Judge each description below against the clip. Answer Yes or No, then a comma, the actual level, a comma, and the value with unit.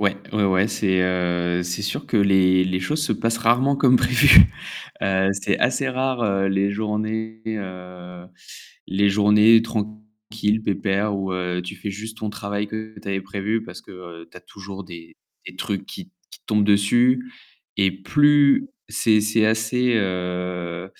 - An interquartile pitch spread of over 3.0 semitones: No, average, 2.7 semitones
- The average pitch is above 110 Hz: No, low, 100 Hz